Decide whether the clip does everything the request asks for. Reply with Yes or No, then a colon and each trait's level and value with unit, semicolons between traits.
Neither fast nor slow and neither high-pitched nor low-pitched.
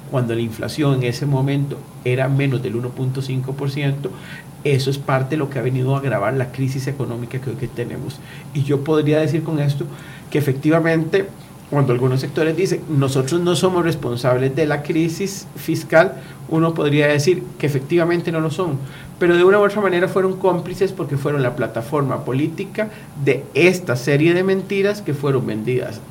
Yes: average, 175 wpm; medium, 145 Hz